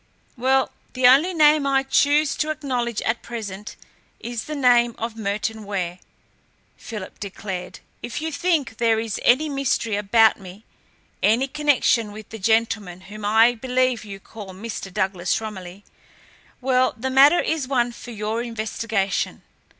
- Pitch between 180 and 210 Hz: No, high, 230 Hz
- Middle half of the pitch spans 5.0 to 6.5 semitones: No, average, 4.0 semitones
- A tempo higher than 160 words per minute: No, average, 145 wpm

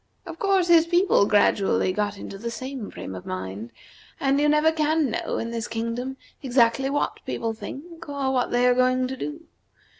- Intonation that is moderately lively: Yes, average, 4.9 semitones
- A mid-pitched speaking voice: No, very high, 255 Hz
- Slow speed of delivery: No, average, 185 wpm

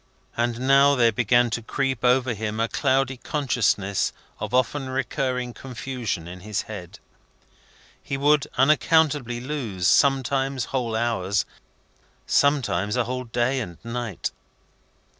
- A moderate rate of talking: No, slow, 120 wpm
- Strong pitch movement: No, average, 3.1 semitones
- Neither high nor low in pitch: No, low, 125 Hz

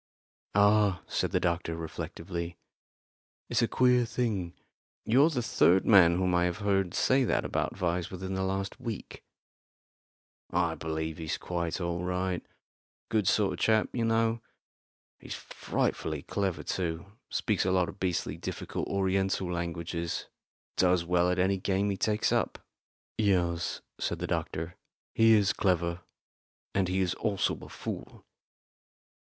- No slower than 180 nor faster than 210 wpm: No, average, 145 wpm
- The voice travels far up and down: No, average, 2.9 semitones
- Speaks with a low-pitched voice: Yes, very low, 95 Hz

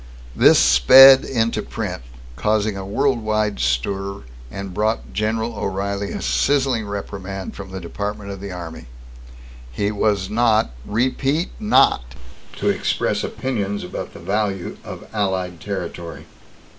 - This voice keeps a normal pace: No, slow, 130 wpm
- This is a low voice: Yes, low, 100 Hz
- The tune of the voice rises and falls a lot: No, narrow, 2.6 semitones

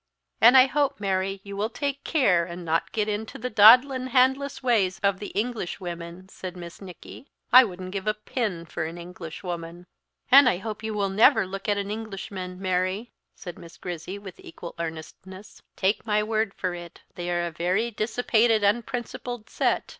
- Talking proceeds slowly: No, average, 180 wpm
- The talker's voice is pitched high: Yes, high, 200 Hz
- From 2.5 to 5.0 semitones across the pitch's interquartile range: Yes, average, 4.0 semitones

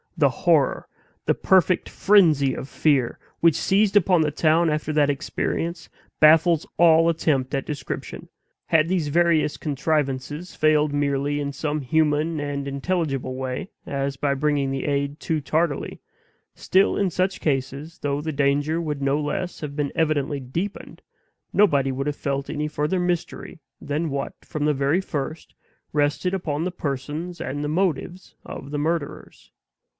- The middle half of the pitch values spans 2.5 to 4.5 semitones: Yes, average, 3.0 semitones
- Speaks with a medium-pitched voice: Yes, medium, 150 Hz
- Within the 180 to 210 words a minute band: No, average, 150 wpm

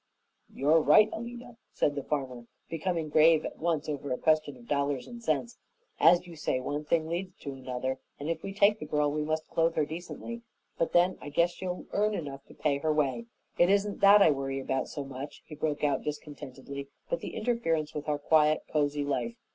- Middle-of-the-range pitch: Yes, medium, 155 Hz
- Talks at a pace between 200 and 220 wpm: Yes, fast, 205 wpm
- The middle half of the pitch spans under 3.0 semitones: No, average, 3.5 semitones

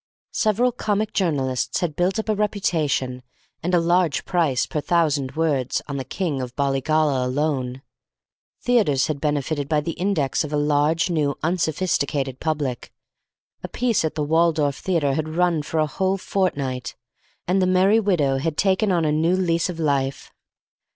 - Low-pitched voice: No, medium, 155 Hz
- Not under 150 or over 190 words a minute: Yes, average, 165 wpm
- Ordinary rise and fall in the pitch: Yes, average, 4.3 semitones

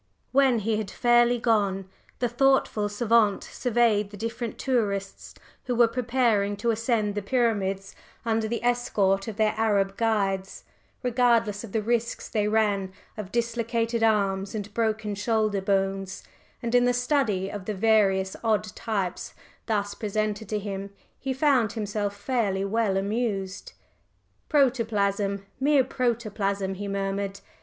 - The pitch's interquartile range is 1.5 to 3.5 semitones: Yes, average, 2.9 semitones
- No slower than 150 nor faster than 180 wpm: No, slow, 135 wpm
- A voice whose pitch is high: Yes, high, 215 Hz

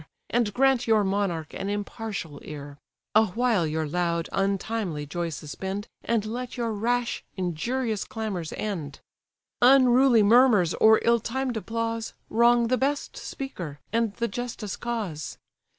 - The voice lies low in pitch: No, high, 220 Hz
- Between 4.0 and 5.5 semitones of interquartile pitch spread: Yes, average, 5.1 semitones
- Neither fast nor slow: No, slow, 130 wpm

